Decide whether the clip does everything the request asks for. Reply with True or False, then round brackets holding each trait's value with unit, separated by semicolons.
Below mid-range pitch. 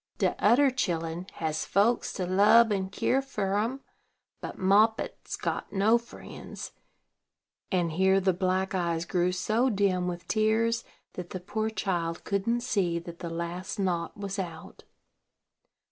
False (190 Hz)